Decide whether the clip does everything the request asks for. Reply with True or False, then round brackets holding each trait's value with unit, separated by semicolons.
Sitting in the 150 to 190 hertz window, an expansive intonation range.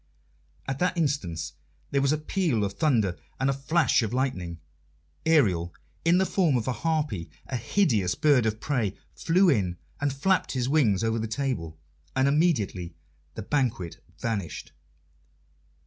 False (130 Hz; 7.1 semitones)